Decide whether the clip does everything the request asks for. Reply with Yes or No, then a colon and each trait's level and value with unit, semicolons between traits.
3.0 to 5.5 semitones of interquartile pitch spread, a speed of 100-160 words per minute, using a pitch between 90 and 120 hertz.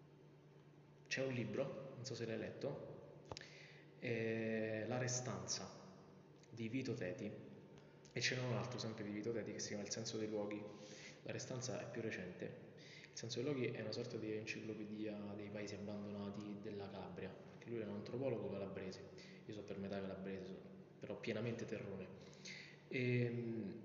No: narrow, 2.4 semitones; average, 155 wpm; low, 110 Hz